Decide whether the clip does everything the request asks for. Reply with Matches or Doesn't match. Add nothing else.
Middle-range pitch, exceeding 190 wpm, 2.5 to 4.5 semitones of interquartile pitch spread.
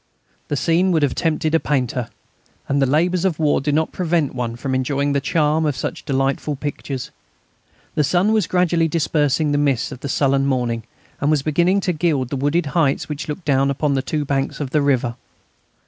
Matches